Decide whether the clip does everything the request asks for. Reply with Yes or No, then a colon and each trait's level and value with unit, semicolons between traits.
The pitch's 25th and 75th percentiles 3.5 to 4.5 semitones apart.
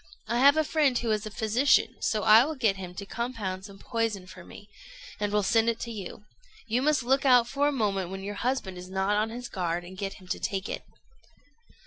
Yes: average, 4.1 semitones